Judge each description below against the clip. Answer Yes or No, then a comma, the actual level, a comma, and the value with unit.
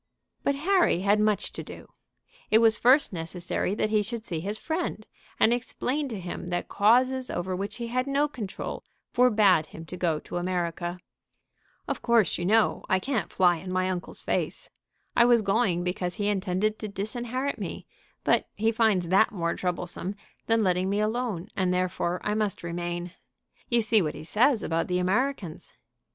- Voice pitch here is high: Yes, high, 205 Hz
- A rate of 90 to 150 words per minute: No, average, 175 wpm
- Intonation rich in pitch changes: No, average, 4.5 semitones